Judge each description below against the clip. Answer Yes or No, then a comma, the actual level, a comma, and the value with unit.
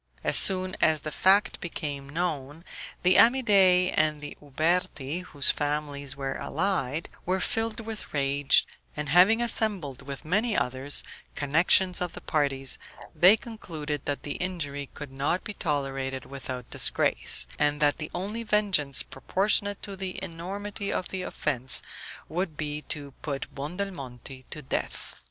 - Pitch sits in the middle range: Yes, medium, 155 Hz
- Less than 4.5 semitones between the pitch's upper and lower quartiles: No, average, 5.0 semitones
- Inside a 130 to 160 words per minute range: Yes, average, 140 wpm